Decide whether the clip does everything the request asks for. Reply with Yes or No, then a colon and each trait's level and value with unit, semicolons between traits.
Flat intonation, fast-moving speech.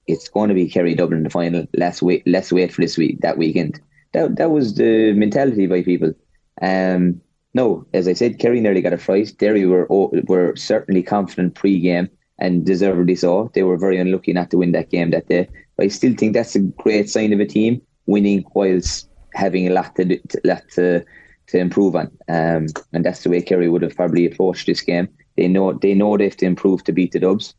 Yes: narrow, 2.0 semitones; fast, 220 wpm